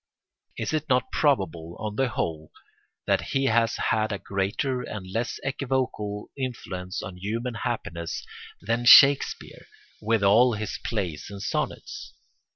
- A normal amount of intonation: Yes, average, 4.3 semitones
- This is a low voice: Yes, low, 110 Hz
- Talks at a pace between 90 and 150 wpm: Yes, slow, 135 wpm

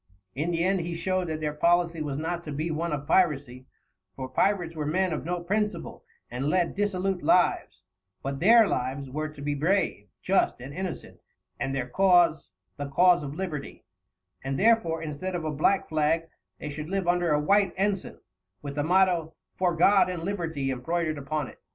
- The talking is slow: No, average, 185 wpm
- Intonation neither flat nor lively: Yes, average, 3.9 semitones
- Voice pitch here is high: No, medium, 165 Hz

